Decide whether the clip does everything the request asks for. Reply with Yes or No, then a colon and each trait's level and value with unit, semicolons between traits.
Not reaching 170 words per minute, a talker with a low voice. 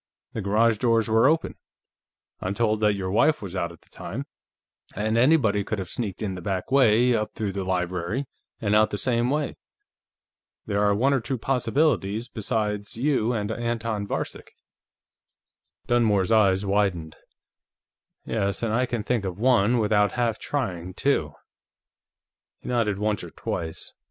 Yes: average, 155 wpm; low, 110 Hz